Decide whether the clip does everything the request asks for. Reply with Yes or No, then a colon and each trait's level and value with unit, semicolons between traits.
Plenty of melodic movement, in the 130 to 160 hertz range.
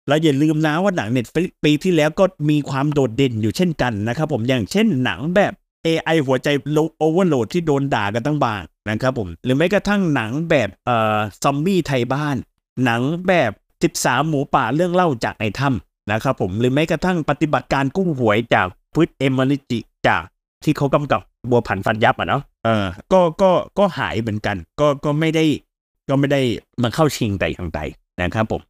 Yes: wide, 5.7 semitones; medium, 140 Hz